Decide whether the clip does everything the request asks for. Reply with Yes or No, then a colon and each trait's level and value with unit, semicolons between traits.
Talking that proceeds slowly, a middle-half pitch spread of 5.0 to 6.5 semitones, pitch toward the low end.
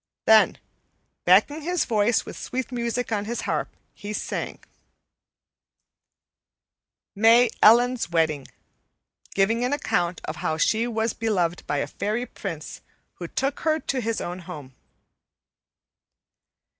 No: slow, 120 wpm; wide, 5.5 semitones; high, 220 Hz